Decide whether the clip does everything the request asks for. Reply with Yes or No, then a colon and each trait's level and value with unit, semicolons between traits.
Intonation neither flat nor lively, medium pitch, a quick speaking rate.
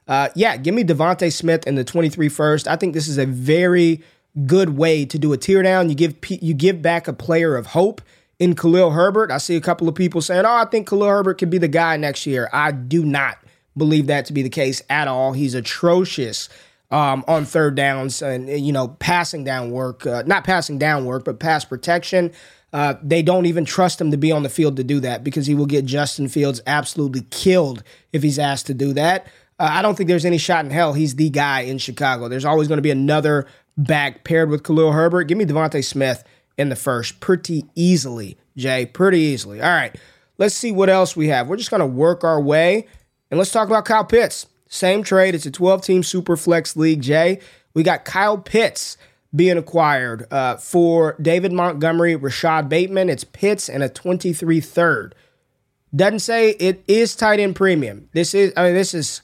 Yes: average, 4.2 semitones; medium, 160 Hz; fast, 210 wpm